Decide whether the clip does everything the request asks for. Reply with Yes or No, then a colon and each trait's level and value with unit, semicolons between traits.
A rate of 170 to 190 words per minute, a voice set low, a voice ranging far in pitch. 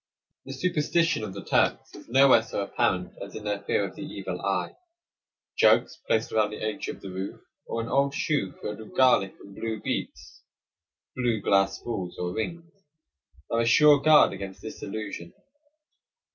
Yes: average, 175 wpm; low, 110 Hz; wide, 5.7 semitones